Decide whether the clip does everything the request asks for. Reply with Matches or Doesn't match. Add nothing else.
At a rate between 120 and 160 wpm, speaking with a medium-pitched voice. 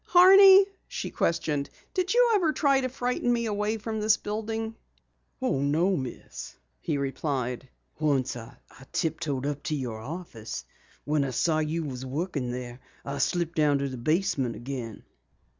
Matches